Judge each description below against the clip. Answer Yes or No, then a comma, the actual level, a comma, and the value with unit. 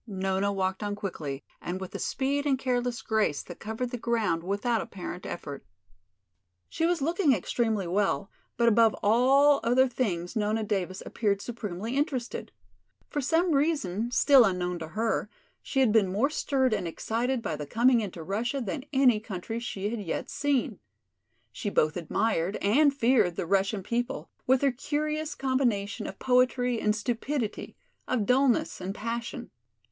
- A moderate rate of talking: Yes, average, 160 wpm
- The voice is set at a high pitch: Yes, high, 225 Hz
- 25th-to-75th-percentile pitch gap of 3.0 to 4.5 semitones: No, average, 4.9 semitones